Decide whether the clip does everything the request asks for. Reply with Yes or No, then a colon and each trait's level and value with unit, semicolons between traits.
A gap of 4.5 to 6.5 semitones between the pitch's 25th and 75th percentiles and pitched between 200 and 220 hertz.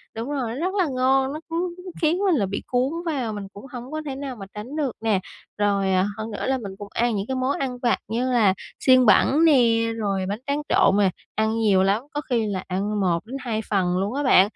No: average, 4.8 semitones; high, 235 Hz